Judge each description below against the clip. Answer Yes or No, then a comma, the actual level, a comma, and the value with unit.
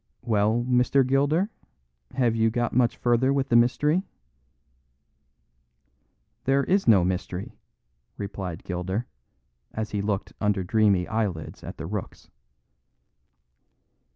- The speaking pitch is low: Yes, low, 110 Hz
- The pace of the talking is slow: Yes, slow, 110 wpm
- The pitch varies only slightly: No, average, 4.3 semitones